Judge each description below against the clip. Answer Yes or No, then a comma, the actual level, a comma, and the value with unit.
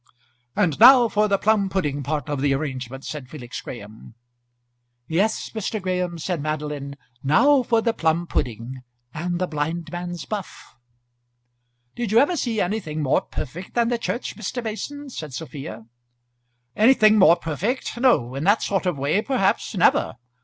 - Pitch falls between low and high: Yes, medium, 175 Hz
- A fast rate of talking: No, average, 155 wpm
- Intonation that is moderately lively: No, wide, 6.9 semitones